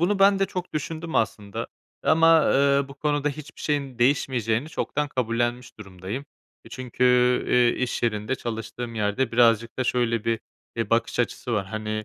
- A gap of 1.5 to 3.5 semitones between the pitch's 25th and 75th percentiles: No, average, 4.0 semitones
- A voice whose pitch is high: No, low, 120 Hz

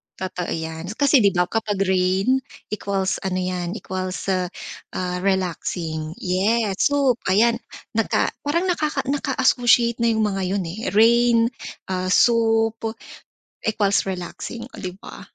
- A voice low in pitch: No, high, 200 Hz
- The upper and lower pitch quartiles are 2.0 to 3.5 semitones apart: No, average, 4.2 semitones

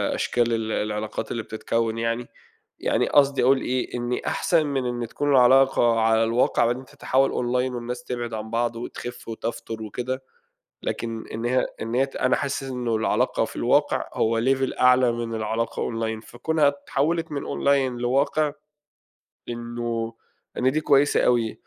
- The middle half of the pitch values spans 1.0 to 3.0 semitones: Yes, narrow, 2.5 semitones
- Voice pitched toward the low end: Yes, low, 120 Hz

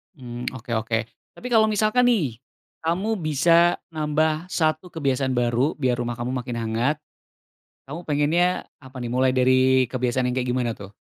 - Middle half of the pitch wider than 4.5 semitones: Yes, average, 4.9 semitones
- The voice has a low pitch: Yes, low, 130 Hz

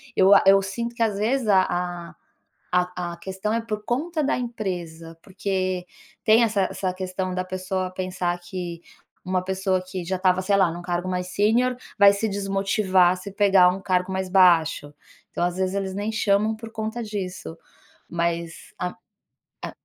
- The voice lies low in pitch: No, high, 190 Hz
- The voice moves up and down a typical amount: No, narrow, 2.1 semitones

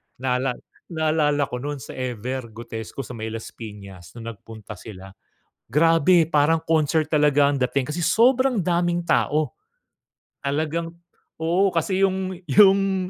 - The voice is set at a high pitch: No, medium, 150 Hz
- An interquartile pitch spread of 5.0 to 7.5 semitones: Yes, wide, 5.6 semitones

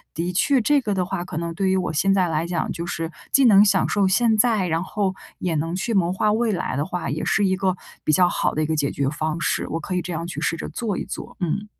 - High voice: No, medium, 180 Hz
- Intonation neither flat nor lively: Yes, average, 3.4 semitones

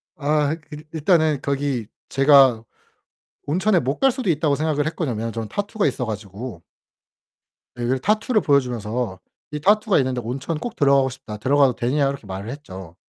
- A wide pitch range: No, average, 4.5 semitones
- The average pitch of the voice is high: No, medium, 140 Hz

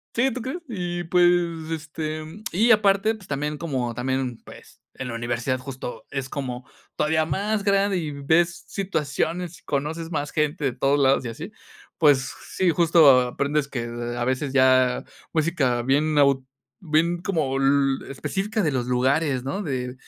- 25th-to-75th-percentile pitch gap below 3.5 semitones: No, average, 4.7 semitones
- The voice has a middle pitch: Yes, medium, 145 Hz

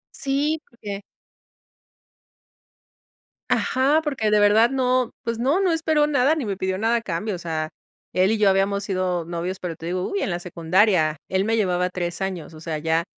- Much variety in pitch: Yes, wide, 5.9 semitones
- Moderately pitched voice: No, high, 200 Hz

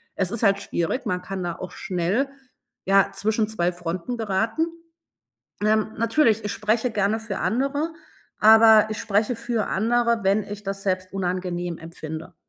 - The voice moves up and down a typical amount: Yes, average, 3.3 semitones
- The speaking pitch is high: Yes, high, 210 Hz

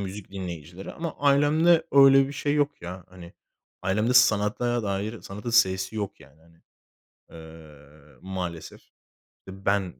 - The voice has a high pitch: No, low, 100 Hz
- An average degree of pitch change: No, wide, 6.0 semitones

